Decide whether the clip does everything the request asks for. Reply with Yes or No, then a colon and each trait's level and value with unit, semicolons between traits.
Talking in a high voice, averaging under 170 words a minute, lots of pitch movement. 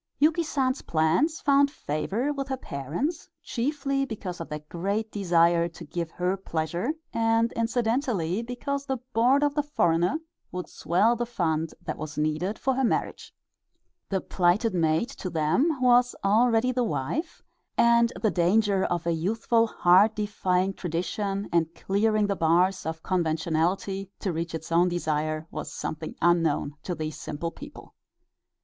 Yes: high, 195 Hz; average, 150 wpm; wide, 6.2 semitones